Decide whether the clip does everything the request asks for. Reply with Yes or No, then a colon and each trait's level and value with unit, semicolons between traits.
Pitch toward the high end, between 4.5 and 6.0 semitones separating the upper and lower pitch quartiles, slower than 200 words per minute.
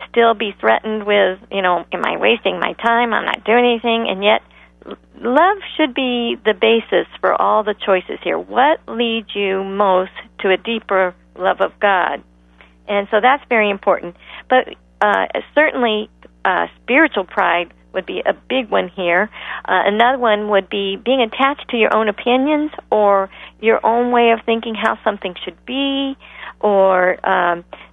No: high, 215 Hz; average, 3.8 semitones; average, 165 wpm